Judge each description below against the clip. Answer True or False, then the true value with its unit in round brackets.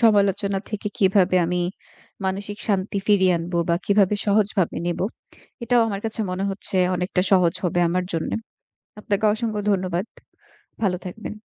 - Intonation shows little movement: True (2.3 semitones)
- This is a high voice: True (195 Hz)